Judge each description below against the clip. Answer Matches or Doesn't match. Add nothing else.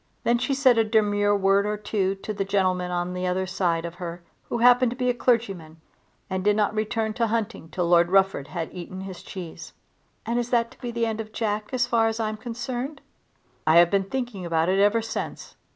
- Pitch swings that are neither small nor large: Matches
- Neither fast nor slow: Doesn't match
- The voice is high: Matches